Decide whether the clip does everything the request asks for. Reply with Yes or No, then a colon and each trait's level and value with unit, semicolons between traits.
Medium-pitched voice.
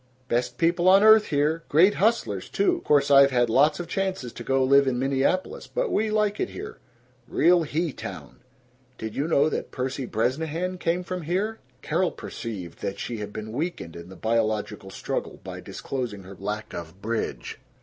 Yes: medium, 145 Hz